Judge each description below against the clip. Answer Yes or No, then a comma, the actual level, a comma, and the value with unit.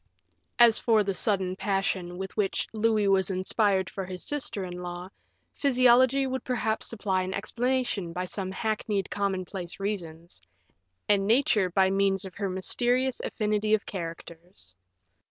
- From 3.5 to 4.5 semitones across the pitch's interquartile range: No, average, 3.0 semitones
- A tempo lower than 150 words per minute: Yes, average, 140 wpm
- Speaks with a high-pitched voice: Yes, high, 195 Hz